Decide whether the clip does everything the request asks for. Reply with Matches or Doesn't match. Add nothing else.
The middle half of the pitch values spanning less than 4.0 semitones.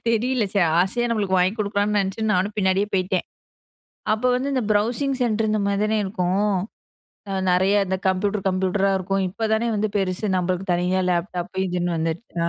Matches